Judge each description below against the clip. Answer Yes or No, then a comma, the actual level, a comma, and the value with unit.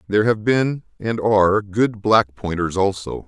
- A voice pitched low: Yes, low, 105 Hz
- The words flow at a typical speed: Yes, average, 165 wpm